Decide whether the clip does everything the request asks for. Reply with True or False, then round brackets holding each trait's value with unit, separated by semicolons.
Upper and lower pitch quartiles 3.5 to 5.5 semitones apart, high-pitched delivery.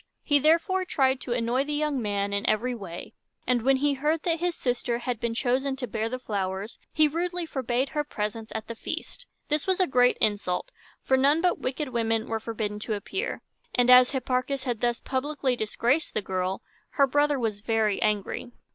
True (4.6 semitones; 250 Hz)